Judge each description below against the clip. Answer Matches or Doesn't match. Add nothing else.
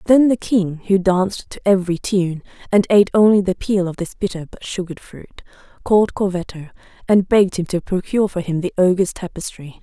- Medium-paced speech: Matches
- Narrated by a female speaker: Matches